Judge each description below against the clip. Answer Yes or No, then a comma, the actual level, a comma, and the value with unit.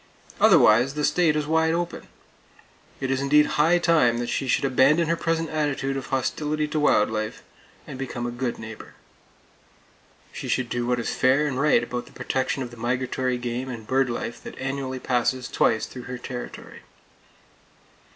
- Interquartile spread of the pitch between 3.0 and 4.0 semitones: Yes, average, 3.5 semitones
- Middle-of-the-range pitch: No, low, 130 Hz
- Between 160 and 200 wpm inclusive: Yes, average, 175 wpm